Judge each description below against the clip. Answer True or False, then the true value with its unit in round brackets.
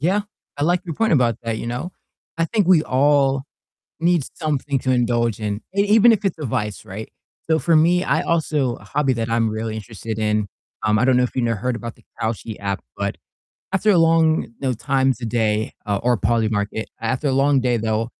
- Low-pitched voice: True (125 Hz)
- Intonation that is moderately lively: False (6.0 semitones)